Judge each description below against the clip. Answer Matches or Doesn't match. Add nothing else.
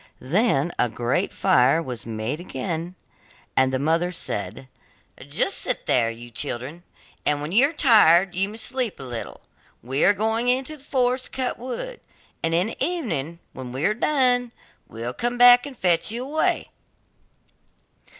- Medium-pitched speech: Matches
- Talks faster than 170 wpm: Doesn't match